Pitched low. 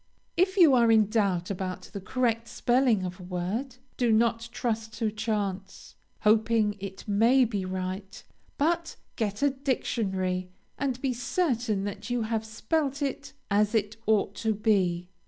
No: high, 220 Hz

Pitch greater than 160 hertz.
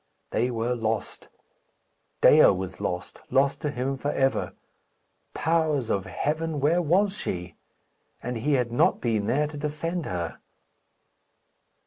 No: low, 135 Hz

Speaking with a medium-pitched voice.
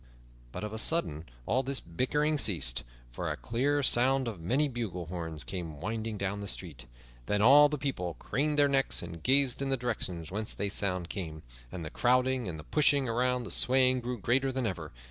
No: low, 115 Hz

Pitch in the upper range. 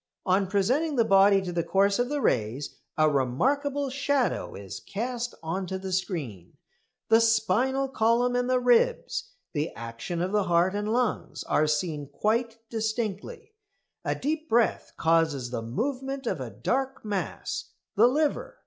Yes: high, 215 Hz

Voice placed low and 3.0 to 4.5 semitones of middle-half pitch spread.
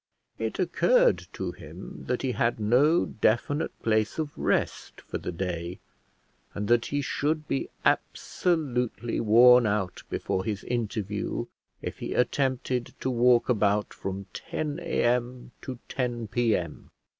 Yes: low, 120 Hz; average, 3.8 semitones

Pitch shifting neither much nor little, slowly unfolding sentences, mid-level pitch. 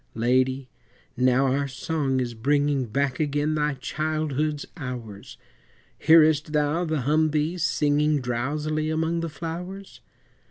Yes: average, 3.0 semitones; slow, 115 wpm; medium, 150 Hz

